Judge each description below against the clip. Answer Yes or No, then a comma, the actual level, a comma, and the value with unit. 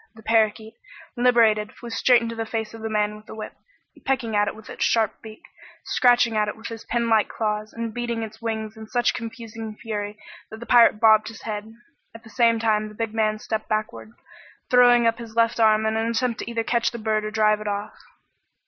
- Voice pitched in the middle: No, high, 220 Hz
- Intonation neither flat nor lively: No, narrow, 1.4 semitones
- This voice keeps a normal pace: No, fast, 220 wpm